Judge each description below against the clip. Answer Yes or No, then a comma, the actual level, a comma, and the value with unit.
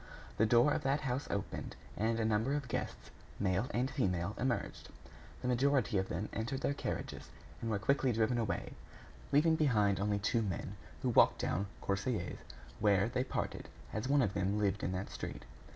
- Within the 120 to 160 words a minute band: No, average, 180 wpm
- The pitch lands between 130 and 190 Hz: No, low, 110 Hz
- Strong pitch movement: No, average, 4.5 semitones